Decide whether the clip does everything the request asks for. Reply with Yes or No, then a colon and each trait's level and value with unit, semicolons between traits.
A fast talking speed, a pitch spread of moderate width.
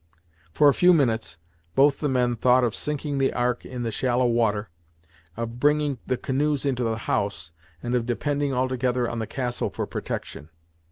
No: average, 175 wpm; average, 3.0 semitones